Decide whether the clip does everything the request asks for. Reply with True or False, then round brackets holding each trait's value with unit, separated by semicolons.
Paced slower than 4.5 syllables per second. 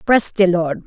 True (4.0 syllables/s)